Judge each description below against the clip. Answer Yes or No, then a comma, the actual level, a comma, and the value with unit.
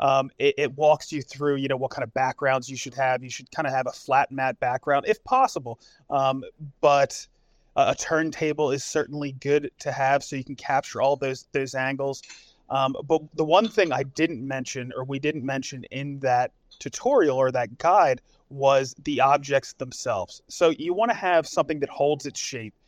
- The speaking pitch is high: No, medium, 140 Hz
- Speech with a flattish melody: Yes, narrow, 2.2 semitones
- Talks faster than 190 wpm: Yes, average, 200 wpm